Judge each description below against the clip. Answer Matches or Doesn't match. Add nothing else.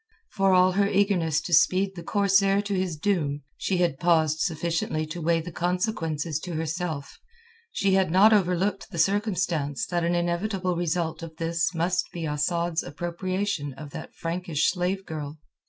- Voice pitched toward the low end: Doesn't match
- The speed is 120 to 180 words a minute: Matches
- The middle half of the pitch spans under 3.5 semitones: Matches